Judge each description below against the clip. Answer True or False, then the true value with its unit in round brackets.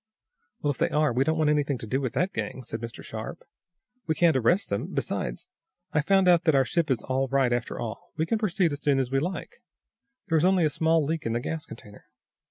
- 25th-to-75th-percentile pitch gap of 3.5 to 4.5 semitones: True (4.2 semitones)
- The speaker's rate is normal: False (240 wpm)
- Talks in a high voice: False (150 Hz)